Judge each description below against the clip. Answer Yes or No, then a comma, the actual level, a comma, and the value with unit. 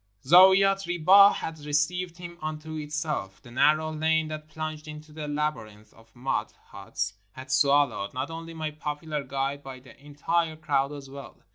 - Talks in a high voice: No, medium, 150 Hz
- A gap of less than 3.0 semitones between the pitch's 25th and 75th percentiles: Yes, narrow, 2.6 semitones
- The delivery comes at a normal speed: Yes, average, 165 wpm